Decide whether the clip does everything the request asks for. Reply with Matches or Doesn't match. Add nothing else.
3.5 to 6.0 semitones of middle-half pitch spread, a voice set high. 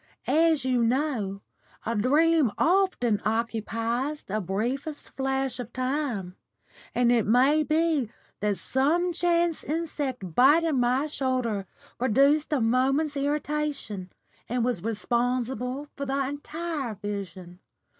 Matches